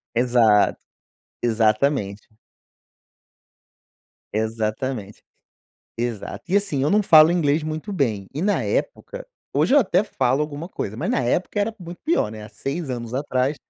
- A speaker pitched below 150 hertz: Yes, low, 135 Hz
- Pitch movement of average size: No, wide, 7.4 semitones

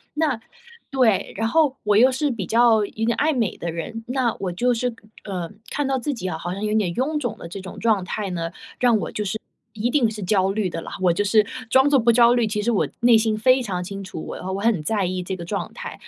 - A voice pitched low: No, high, 220 Hz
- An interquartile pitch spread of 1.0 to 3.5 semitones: No, average, 4.2 semitones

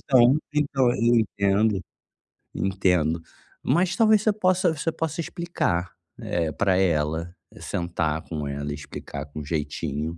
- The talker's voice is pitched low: Yes, very low, 95 Hz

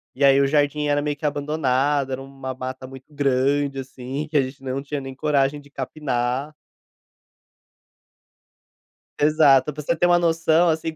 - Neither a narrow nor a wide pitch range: No, narrow, 2.1 semitones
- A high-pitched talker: No, medium, 140 Hz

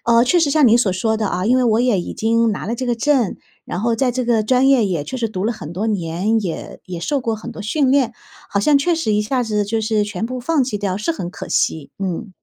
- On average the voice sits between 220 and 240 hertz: Yes, high, 225 Hz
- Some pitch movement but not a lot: Yes, average, 3.7 semitones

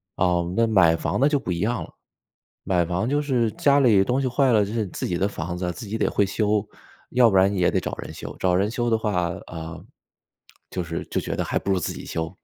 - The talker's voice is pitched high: No, low, 100 Hz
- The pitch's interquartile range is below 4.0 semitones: No, average, 4.7 semitones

